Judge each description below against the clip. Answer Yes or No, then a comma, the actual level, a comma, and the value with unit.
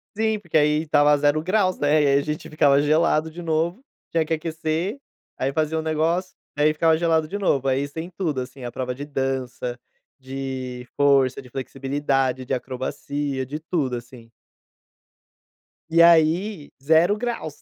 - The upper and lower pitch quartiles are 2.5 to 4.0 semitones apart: Yes, average, 3.4 semitones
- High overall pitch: No, medium, 150 Hz